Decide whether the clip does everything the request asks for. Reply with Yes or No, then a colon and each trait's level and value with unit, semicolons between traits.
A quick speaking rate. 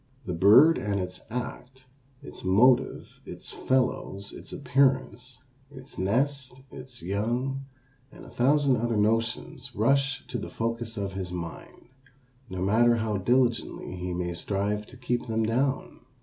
No: average, 140 wpm